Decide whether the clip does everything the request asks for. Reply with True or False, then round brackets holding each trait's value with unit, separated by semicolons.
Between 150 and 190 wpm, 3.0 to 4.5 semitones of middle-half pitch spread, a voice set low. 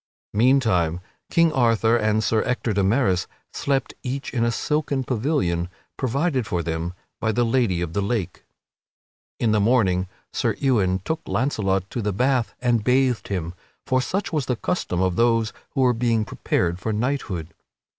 False (165 wpm; 5.3 semitones; 115 Hz)